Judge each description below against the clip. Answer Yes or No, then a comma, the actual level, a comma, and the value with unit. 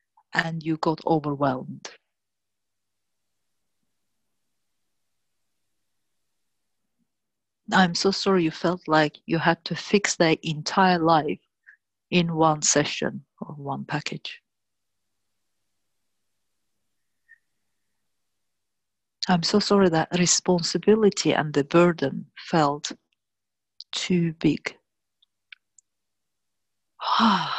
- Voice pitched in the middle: Yes, medium, 145 Hz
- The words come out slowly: Yes, slow, 75 wpm